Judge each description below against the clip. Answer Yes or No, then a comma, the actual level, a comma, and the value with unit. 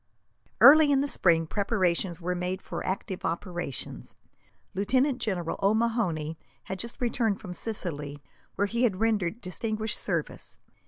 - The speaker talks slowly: Yes, slow, 130 wpm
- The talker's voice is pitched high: Yes, high, 195 Hz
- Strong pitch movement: No, average, 4.6 semitones